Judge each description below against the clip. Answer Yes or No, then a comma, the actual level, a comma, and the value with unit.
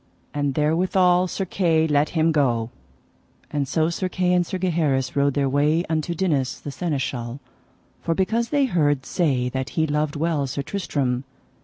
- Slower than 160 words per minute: No, average, 165 wpm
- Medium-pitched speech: Yes, medium, 155 Hz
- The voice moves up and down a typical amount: Yes, average, 4.0 semitones